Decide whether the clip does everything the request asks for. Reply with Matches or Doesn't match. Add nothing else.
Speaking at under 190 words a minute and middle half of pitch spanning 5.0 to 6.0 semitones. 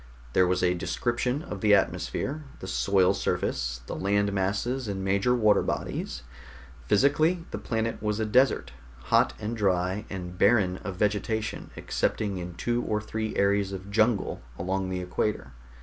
Doesn't match